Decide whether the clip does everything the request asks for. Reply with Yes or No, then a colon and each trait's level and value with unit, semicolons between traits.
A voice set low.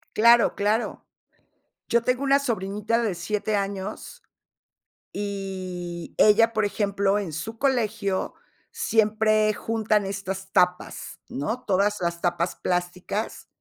No: high, 205 Hz